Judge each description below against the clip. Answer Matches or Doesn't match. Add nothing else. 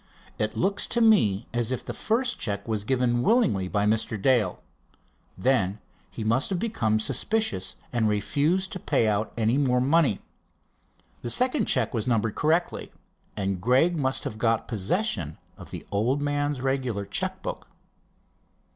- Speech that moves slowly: Doesn't match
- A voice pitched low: Matches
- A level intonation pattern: Doesn't match